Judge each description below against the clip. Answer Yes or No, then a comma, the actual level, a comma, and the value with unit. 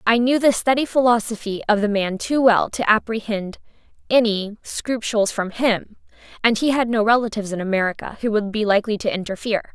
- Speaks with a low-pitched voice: No, high, 220 Hz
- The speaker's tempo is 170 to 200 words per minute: Yes, average, 180 wpm